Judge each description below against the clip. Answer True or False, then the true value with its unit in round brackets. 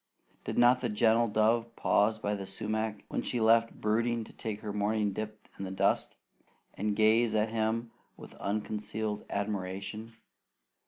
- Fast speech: False (155 wpm)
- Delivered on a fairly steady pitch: True (1.6 semitones)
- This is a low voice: True (110 Hz)